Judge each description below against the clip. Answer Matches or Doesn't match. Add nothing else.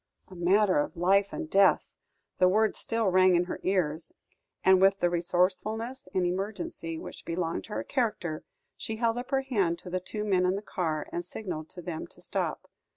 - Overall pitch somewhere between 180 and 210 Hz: Matches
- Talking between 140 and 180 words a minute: Doesn't match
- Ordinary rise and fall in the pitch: Matches